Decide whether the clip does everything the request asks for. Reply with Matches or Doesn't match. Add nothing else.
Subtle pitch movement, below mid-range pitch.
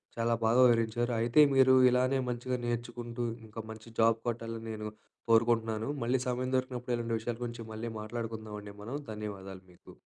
Matches